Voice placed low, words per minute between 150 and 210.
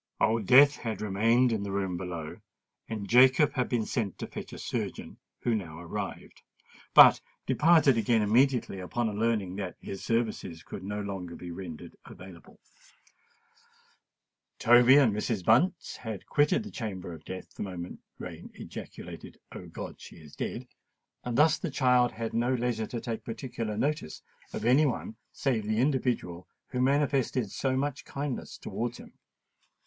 Yes: low, 115 Hz; average, 155 wpm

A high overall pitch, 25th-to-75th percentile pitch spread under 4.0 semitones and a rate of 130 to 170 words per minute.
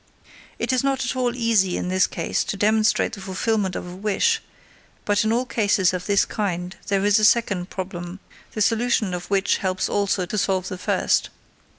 No: high, 200 Hz; average, 3.0 semitones; average, 200 wpm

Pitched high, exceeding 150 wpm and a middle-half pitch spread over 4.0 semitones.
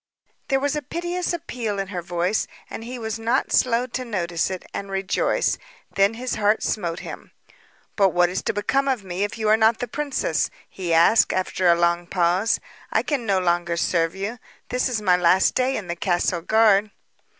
Yes: high, 205 Hz; average, 195 wpm; average, 5.3 semitones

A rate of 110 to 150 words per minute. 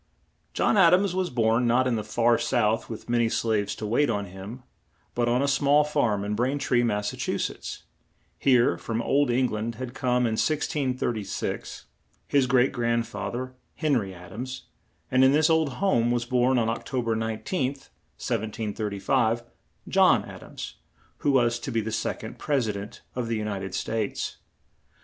No: average, 185 wpm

